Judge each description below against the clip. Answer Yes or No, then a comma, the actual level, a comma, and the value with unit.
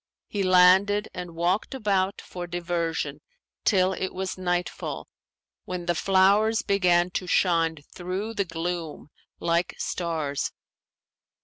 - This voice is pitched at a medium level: Yes, medium, 180 Hz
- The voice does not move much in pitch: Yes, narrow, 2.0 semitones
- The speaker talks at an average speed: No, slow, 115 wpm